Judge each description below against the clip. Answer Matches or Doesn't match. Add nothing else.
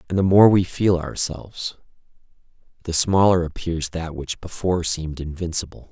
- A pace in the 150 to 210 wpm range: Doesn't match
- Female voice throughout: Doesn't match